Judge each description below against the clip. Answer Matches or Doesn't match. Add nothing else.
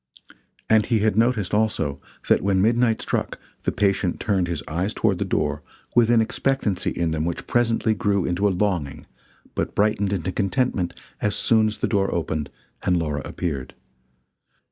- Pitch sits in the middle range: Doesn't match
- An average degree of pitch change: Matches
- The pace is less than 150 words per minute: Doesn't match